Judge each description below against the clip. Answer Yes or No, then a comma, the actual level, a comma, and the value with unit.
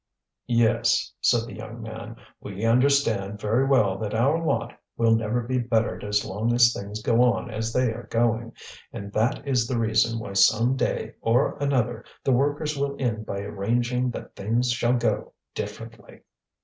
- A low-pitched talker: Yes, low, 115 Hz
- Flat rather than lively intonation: Yes, narrow, 2.3 semitones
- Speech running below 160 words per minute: No, average, 170 wpm